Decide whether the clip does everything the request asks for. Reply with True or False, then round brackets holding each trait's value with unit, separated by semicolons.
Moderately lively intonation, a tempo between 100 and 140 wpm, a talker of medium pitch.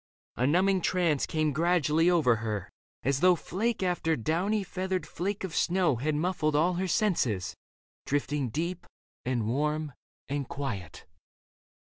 True (4.8 semitones; 135 wpm; 155 Hz)